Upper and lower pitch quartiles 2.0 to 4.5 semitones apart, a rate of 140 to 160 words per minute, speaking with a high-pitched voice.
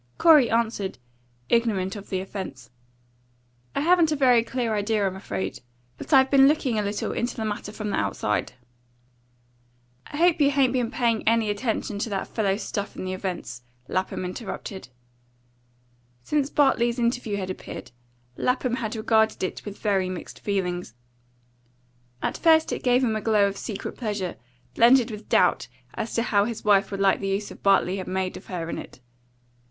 No: average, 3.9 semitones; average, 170 wpm; high, 215 Hz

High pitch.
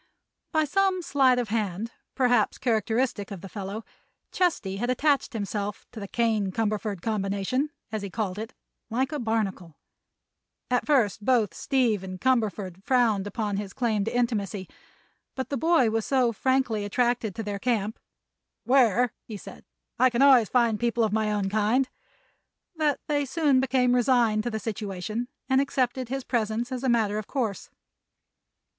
Yes: high, 230 Hz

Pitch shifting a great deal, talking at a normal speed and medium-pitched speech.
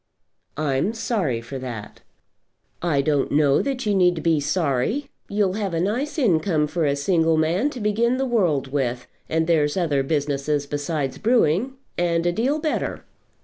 Yes: wide, 6.6 semitones; average, 160 wpm; medium, 165 Hz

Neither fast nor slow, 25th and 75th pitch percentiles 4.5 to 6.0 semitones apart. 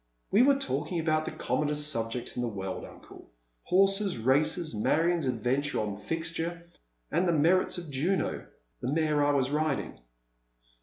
Yes: average, 160 wpm; average, 4.9 semitones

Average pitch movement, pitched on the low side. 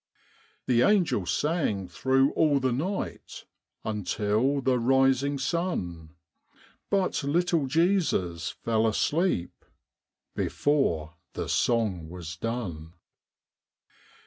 No: wide, 8.2 semitones; low, 125 Hz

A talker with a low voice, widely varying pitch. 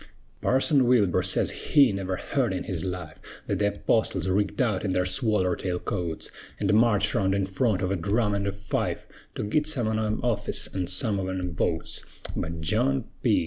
No: low, 100 Hz; average, 3.0 semitones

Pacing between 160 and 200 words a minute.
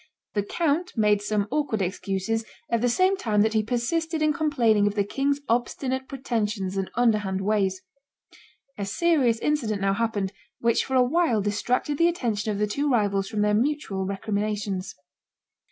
Yes: average, 165 wpm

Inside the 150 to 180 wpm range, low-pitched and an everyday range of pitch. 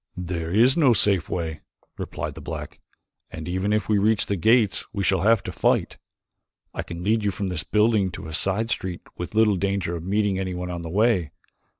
No: fast, 205 wpm; very low, 95 Hz; average, 3.3 semitones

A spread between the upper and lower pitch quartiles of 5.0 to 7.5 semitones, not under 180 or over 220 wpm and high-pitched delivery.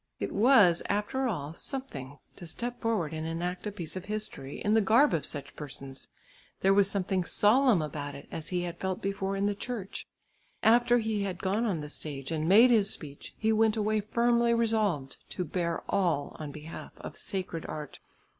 Yes: wide, 5.5 semitones; average, 190 wpm; high, 195 Hz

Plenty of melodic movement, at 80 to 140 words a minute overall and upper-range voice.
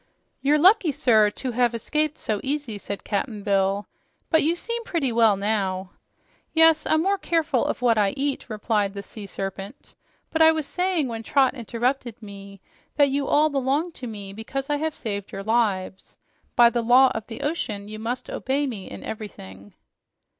No: wide, 6.0 semitones; average, 180 wpm; high, 235 Hz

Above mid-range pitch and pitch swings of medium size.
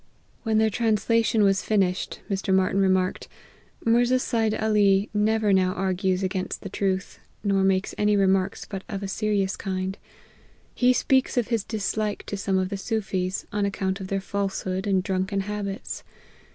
No: high, 195 Hz; narrow, 2.1 semitones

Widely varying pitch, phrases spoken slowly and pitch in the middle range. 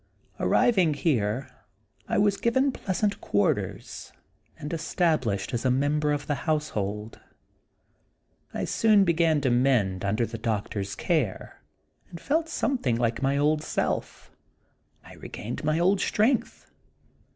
Yes: wide, 7.4 semitones; slow, 125 wpm; medium, 145 Hz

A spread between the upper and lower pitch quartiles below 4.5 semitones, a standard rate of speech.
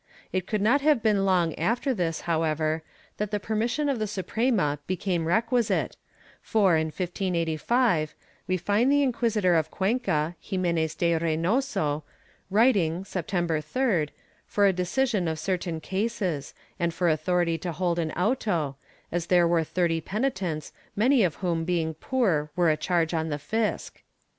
No: average, 4.9 semitones; average, 155 wpm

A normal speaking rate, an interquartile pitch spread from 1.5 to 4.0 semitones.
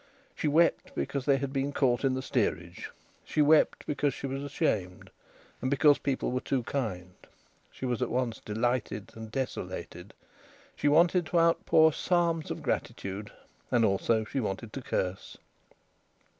No: average, 155 wpm; average, 4.8 semitones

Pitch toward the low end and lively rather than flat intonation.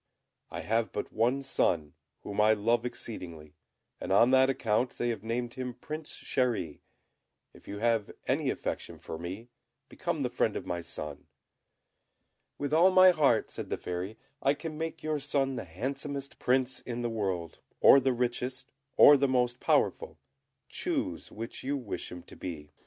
No: low, 120 Hz; average, 4.8 semitones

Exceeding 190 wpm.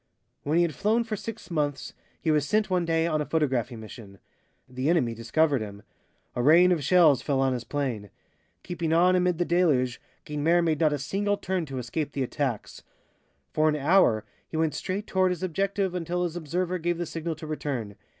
Yes: average, 200 wpm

